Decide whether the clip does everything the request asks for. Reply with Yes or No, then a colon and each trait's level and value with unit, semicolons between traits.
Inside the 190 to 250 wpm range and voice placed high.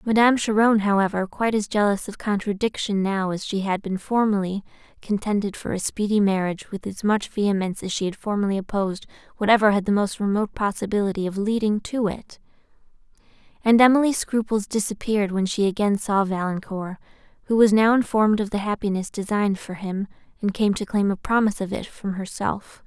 No: average, 175 wpm; high, 205 Hz